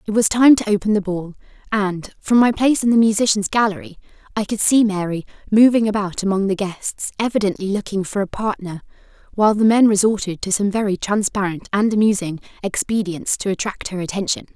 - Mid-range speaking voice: No, high, 205 Hz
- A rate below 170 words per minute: No, average, 180 wpm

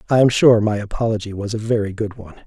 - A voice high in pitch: No, low, 110 Hz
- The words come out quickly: Yes, fast, 245 wpm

